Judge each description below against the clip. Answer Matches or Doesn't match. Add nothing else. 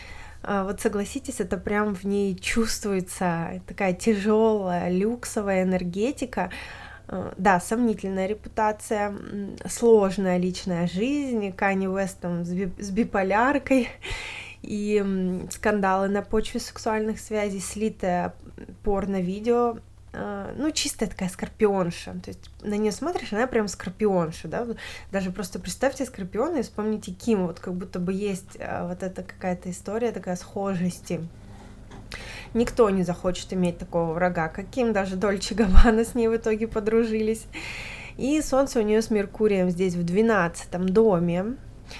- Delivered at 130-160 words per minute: Doesn't match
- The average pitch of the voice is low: Doesn't match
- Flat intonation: Doesn't match